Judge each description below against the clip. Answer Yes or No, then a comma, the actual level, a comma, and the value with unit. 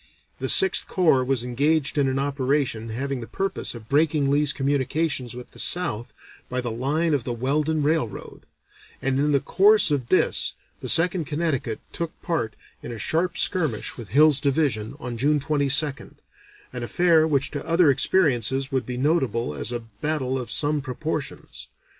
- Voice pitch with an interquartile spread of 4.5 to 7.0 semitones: No, average, 3.9 semitones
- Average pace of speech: Yes, average, 165 wpm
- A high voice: No, medium, 140 Hz